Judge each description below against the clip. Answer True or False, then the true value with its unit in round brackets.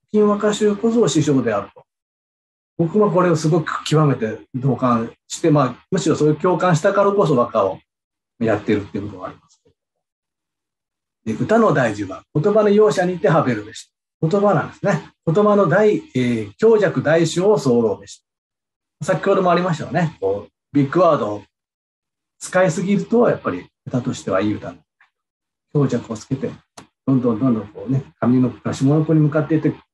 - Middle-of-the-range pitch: True (155 Hz)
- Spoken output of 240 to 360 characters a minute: True (335 characters per minute)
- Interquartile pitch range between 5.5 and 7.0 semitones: False (7.6 semitones)